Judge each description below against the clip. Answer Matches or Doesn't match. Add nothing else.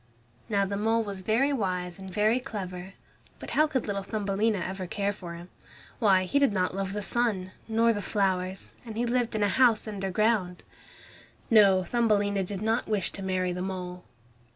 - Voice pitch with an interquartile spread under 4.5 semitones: Matches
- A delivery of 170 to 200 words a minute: Matches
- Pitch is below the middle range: Doesn't match